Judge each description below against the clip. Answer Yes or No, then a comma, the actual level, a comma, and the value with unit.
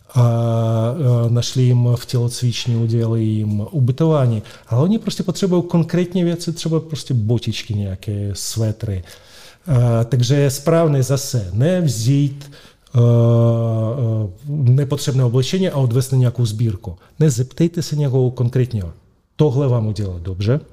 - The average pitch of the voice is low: Yes, low, 125 Hz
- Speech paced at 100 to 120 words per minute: Yes, slow, 115 wpm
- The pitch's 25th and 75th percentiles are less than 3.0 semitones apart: No, average, 4.1 semitones